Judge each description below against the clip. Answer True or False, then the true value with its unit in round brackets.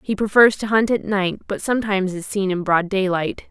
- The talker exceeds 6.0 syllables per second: False (5.5 syllables/s)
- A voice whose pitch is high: True (200 Hz)